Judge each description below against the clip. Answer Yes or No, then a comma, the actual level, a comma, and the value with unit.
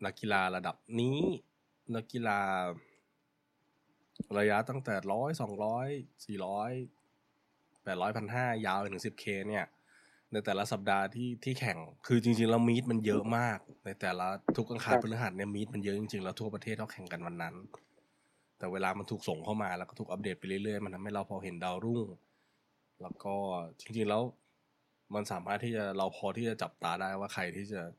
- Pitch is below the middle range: Yes, low, 105 Hz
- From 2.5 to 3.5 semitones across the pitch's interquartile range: Yes, average, 3.2 semitones